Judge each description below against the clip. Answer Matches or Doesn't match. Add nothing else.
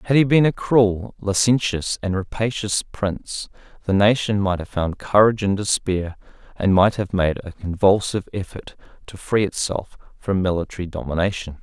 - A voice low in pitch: Matches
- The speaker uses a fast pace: Doesn't match